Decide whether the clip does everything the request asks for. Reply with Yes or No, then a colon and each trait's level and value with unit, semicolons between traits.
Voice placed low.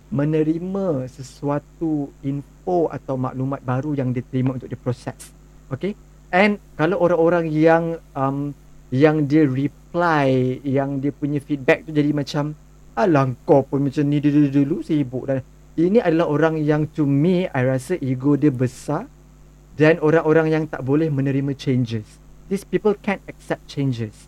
No: medium, 150 Hz